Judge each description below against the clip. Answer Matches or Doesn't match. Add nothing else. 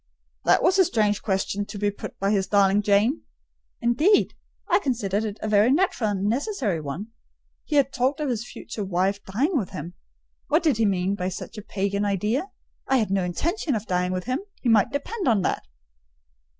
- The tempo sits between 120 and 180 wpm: Doesn't match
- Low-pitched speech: Doesn't match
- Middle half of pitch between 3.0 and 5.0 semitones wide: Doesn't match